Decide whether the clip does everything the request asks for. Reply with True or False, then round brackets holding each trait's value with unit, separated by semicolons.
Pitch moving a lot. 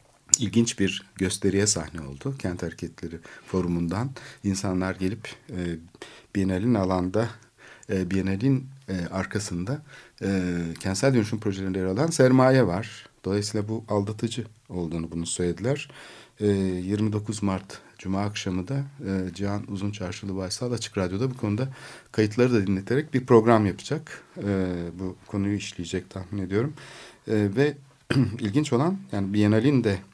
False (4.2 semitones)